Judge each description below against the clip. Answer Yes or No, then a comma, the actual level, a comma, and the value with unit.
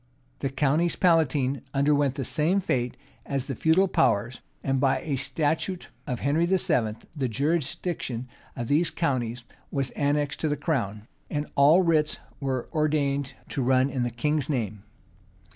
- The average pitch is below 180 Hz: Yes, medium, 140 Hz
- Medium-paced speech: Yes, average, 150 wpm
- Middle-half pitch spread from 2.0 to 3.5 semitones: Yes, average, 3.2 semitones